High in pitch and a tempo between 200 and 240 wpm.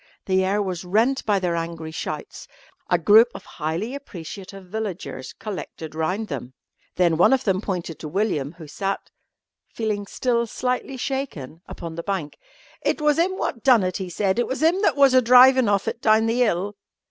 No: high, 200 Hz; average, 185 wpm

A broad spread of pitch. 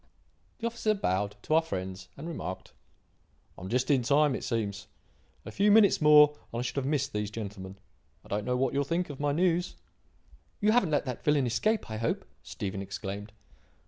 Yes: wide, 7.1 semitones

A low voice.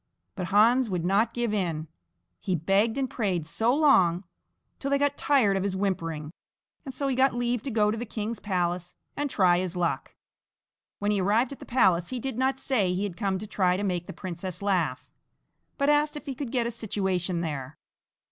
No: high, 205 Hz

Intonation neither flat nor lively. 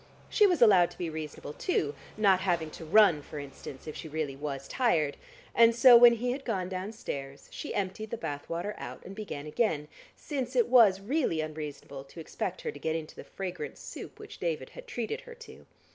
No: wide, 7.4 semitones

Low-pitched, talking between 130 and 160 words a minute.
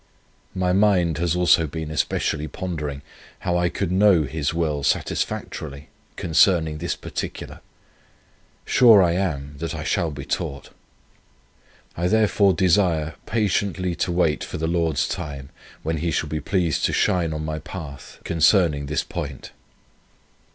Yes: very low, 85 Hz; average, 140 wpm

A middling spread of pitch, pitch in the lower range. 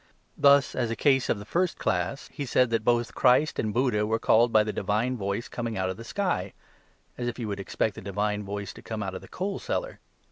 Yes: average, 3.7 semitones; low, 115 Hz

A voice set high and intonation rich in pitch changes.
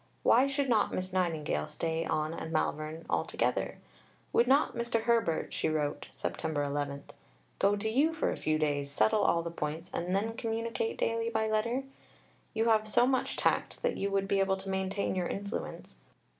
Yes: high, 195 Hz; wide, 6.1 semitones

